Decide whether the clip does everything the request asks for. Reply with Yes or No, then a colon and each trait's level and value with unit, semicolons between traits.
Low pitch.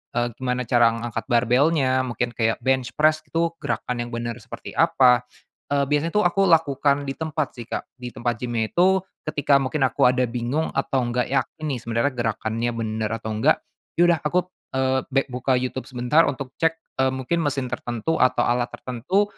Yes: low, 130 Hz